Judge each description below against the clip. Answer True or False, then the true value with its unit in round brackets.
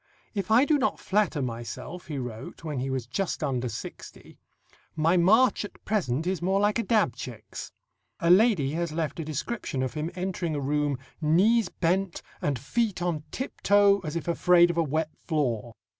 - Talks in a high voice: False (165 Hz)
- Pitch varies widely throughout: True (5.8 semitones)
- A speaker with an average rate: True (180 wpm)